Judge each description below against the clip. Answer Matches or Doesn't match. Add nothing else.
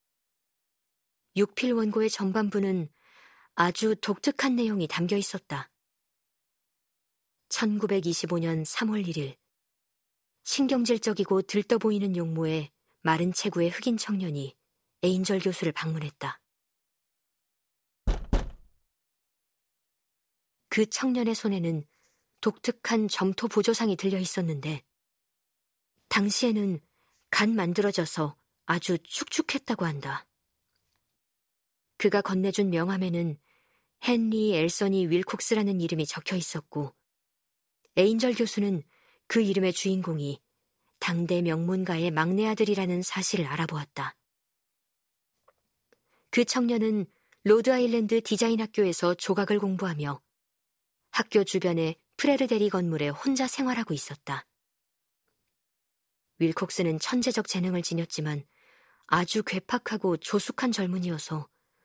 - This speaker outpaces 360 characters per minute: Doesn't match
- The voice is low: Doesn't match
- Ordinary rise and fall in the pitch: Matches